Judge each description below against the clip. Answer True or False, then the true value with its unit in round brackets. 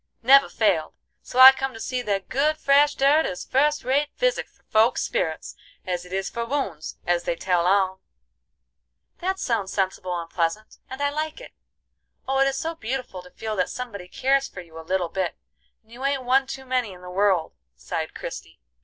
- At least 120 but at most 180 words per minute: False (200 wpm)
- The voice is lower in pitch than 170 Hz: False (230 Hz)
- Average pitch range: False (6.8 semitones)